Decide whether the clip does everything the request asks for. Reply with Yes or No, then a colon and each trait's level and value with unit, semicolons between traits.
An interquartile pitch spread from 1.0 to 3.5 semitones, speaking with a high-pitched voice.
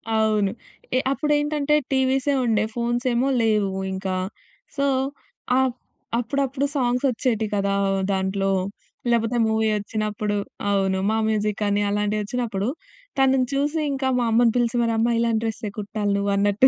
No: average, 3.9 semitones; high, 225 Hz